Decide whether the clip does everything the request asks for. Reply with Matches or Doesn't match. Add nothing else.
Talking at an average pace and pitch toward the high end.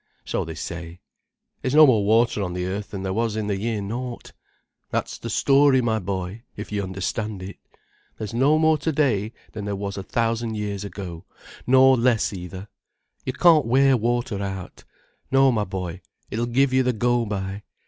Doesn't match